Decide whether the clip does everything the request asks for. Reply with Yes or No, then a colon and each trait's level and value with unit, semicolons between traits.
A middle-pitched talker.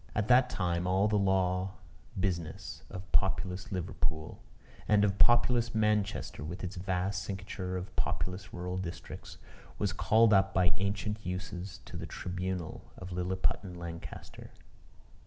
No: very low, 95 Hz